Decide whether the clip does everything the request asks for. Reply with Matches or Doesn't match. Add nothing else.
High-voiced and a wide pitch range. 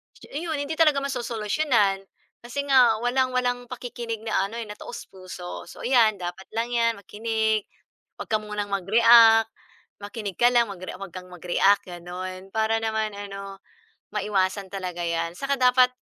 Doesn't match